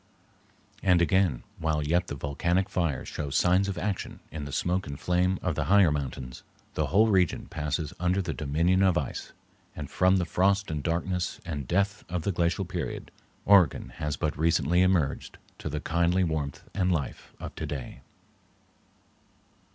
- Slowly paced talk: No, average, 165 wpm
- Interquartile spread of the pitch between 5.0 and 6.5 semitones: No, average, 3.7 semitones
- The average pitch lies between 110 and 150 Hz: No, very low, 85 Hz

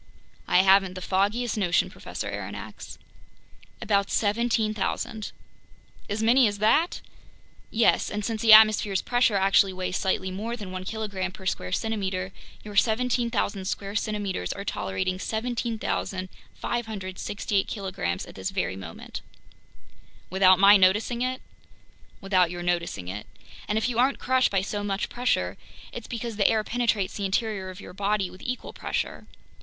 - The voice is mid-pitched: No, high, 205 Hz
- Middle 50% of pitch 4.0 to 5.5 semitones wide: No, average, 3.0 semitones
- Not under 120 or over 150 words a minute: Yes, average, 145 wpm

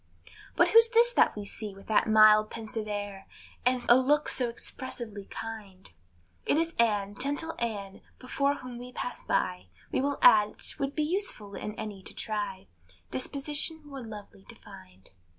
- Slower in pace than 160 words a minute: No, average, 170 wpm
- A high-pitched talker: Yes, high, 225 Hz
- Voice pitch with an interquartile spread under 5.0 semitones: No, average, 5.3 semitones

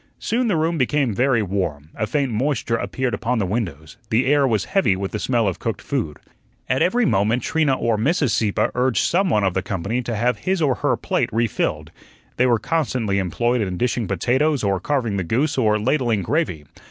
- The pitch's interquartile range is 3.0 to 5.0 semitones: No, wide, 5.4 semitones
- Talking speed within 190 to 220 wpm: Yes, average, 200 wpm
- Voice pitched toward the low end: Yes, low, 120 Hz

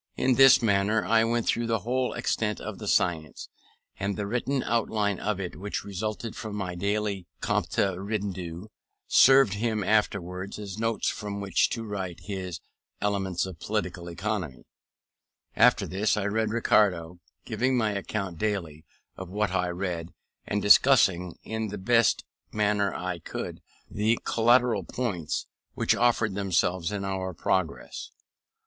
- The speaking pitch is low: Yes, low, 100 Hz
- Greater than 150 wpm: No, average, 145 wpm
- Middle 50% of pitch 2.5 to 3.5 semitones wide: Yes, average, 3.1 semitones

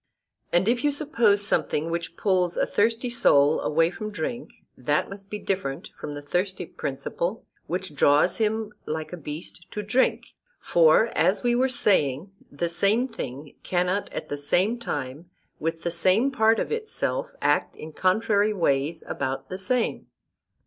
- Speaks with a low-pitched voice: No, medium, 185 Hz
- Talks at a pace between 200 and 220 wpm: No, average, 160 wpm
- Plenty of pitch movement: Yes, wide, 5.9 semitones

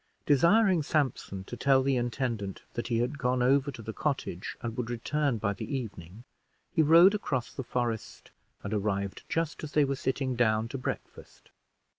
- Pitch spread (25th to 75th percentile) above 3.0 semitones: Yes, average, 4.1 semitones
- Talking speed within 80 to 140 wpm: No, average, 175 wpm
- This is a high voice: No, low, 125 Hz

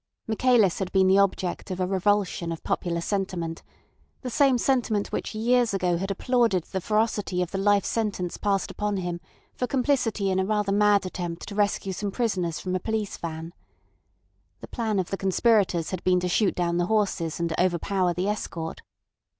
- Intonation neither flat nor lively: Yes, average, 3.0 semitones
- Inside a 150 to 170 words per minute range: No, average, 185 wpm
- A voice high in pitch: Yes, high, 195 Hz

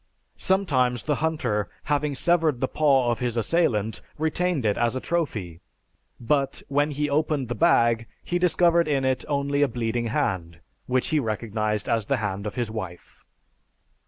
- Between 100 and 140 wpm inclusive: No, average, 160 wpm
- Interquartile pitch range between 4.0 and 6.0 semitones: Yes, average, 5.1 semitones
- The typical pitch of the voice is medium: No, low, 130 Hz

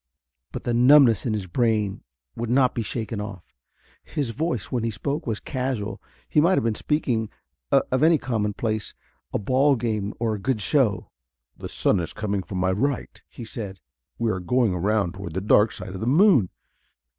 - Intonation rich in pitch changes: No, average, 4.0 semitones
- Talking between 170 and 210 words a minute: Yes, average, 185 wpm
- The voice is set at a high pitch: No, low, 110 Hz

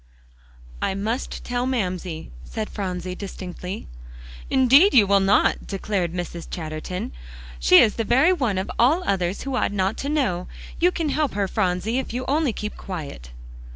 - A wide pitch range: Yes, wide, 5.9 semitones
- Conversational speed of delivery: Yes, average, 160 wpm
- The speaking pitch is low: No, high, 200 Hz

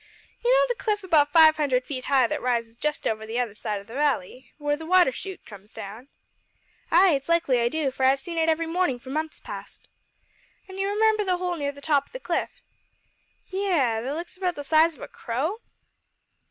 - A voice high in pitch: Yes, very high, 295 Hz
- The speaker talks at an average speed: No, fast, 220 wpm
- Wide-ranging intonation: Yes, wide, 5.9 semitones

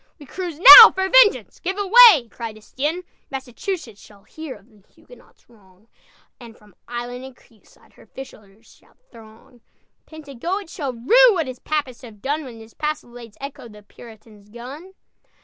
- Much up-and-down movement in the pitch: Yes, wide, 5.9 semitones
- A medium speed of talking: Yes, average, 155 wpm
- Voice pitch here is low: No, very high, 255 Hz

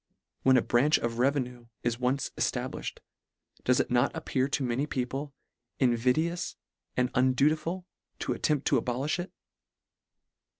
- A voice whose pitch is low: Yes, low, 130 Hz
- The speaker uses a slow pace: Yes, slow, 130 wpm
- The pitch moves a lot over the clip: No, average, 2.9 semitones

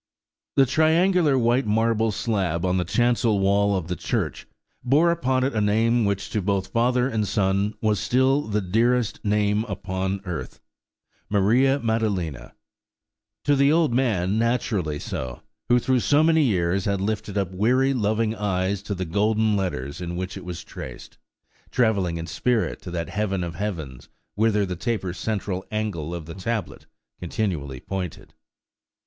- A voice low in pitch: Yes, low, 105 Hz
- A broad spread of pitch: No, average, 4.2 semitones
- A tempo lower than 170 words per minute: Yes, average, 155 wpm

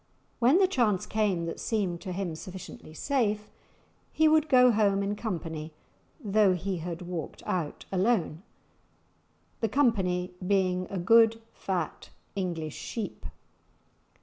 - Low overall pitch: No, high, 195 Hz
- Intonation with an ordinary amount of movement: Yes, average, 4.1 semitones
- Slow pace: Yes, slow, 125 wpm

